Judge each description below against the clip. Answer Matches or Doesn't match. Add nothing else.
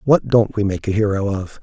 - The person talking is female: Doesn't match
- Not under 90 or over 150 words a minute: Doesn't match